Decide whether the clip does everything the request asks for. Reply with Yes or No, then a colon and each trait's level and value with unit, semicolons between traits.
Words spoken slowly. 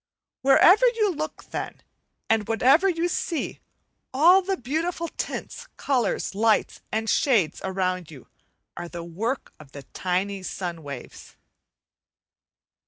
Yes: slow, 120 wpm